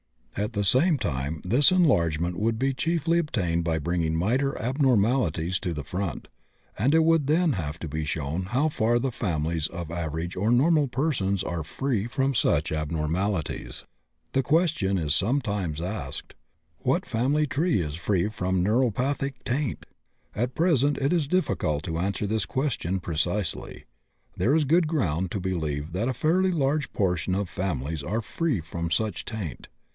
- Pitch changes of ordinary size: No, wide, 8.3 semitones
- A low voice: Yes, low, 105 Hz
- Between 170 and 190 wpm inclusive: No, average, 160 wpm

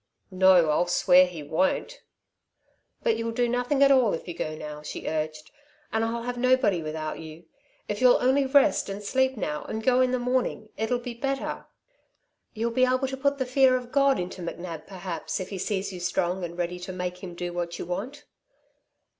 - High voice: Yes, high, 205 Hz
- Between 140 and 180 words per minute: No, average, 200 wpm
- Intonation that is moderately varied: No, wide, 6.4 semitones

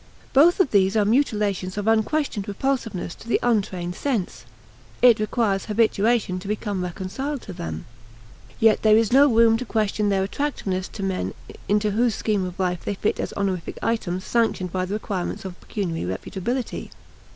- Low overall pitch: No, high, 210 Hz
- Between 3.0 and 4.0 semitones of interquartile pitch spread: Yes, average, 3.5 semitones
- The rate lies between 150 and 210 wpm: Yes, average, 165 wpm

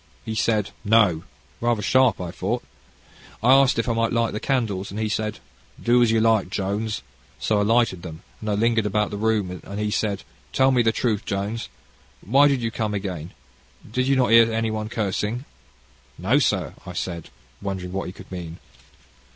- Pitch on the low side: Yes, low, 110 Hz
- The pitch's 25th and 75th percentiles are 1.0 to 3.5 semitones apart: Yes, average, 2.9 semitones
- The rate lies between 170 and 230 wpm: Yes, average, 190 wpm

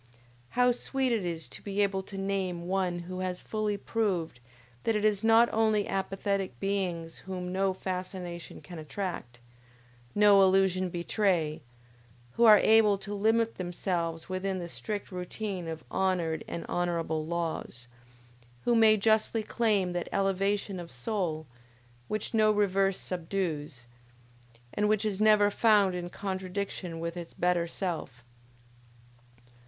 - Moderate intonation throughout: Yes, average, 3.0 semitones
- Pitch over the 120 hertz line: Yes, high, 190 Hz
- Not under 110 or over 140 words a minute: Yes, slow, 135 wpm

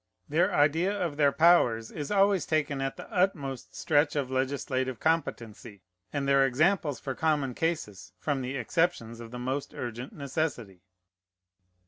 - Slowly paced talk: No, average, 145 wpm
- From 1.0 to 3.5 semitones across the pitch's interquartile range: No, average, 4.2 semitones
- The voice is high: No, medium, 140 Hz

